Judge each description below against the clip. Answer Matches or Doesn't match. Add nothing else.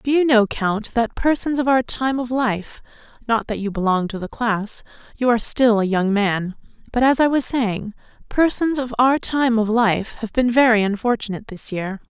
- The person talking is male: Doesn't match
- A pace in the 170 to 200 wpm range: Matches